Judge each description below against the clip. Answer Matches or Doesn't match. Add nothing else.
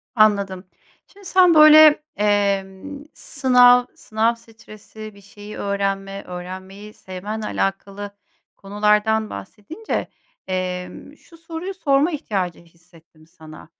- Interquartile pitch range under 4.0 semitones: Doesn't match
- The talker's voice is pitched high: Matches